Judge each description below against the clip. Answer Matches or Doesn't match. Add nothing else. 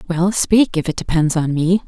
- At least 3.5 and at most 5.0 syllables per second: Matches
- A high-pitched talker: Doesn't match